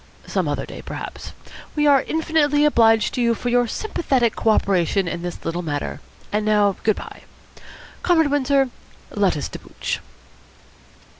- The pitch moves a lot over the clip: Yes, wide, 6.4 semitones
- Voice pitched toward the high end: Yes, high, 235 Hz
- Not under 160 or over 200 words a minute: No, average, 150 wpm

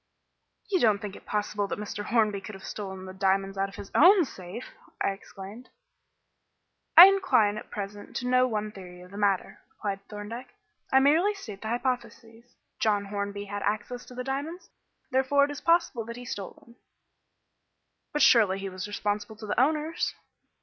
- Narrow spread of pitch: No, average, 4.1 semitones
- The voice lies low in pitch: No, high, 215 Hz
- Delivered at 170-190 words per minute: Yes, average, 175 wpm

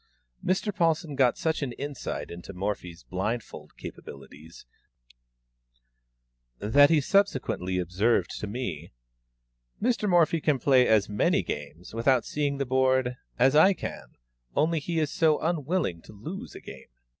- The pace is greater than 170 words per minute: No, slow, 135 wpm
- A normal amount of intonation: No, wide, 7.7 semitones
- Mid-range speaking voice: No, low, 130 Hz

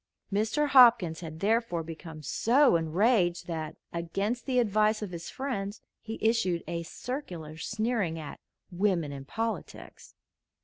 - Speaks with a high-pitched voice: Yes, high, 195 Hz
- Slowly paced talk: Yes, slow, 130 wpm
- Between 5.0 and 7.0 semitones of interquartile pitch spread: Yes, wide, 5.6 semitones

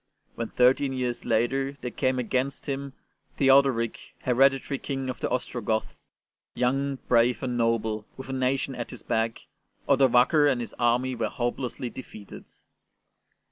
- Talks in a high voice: No, low, 125 Hz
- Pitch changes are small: Yes, narrow, 2.2 semitones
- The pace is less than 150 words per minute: Yes, average, 140 wpm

